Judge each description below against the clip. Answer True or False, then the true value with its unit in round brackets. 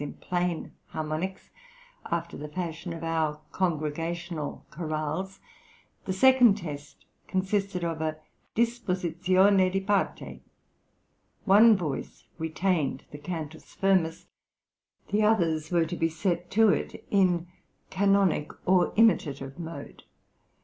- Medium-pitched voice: True (175 Hz)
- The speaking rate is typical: False (110 wpm)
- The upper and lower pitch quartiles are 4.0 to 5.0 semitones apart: False (3.4 semitones)